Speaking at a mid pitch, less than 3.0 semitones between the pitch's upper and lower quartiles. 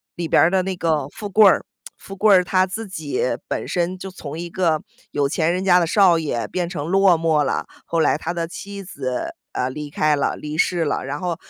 No: medium, 170 Hz; average, 3.5 semitones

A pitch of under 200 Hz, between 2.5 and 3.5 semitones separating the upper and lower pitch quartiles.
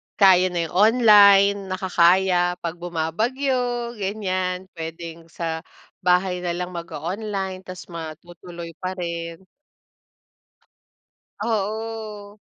Yes: medium, 185 Hz; average, 3.1 semitones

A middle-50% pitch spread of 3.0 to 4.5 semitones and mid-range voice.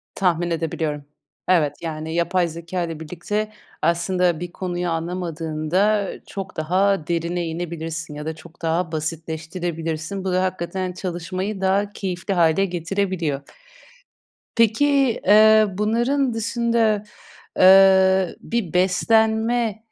Yes: average, 3.4 semitones; medium, 180 Hz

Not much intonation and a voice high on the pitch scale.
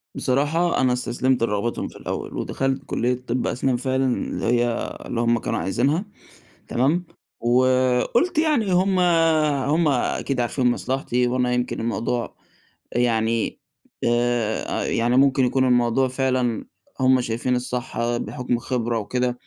No: narrow, 1.8 semitones; low, 125 Hz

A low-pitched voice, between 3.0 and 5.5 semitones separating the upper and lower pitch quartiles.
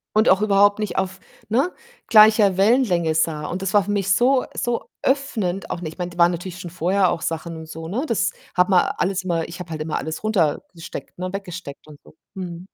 No: medium, 185 Hz; average, 3.4 semitones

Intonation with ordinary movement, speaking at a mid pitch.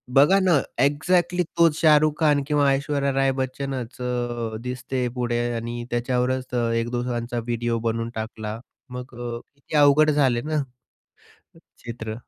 No: average, 3.4 semitones; low, 125 Hz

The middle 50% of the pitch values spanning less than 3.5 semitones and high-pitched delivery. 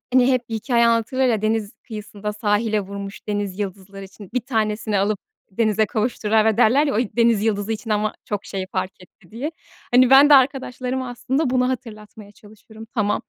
Yes: average, 3.0 semitones; high, 220 Hz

